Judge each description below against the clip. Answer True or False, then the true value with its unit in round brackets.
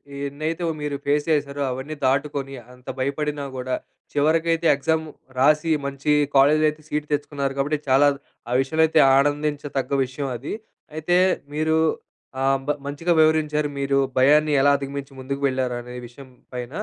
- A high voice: False (145 Hz)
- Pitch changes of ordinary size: False (1.9 semitones)